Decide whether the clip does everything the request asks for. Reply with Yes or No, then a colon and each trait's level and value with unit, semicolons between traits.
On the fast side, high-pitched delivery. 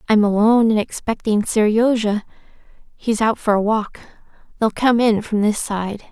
No: average, 155 wpm; high, 215 Hz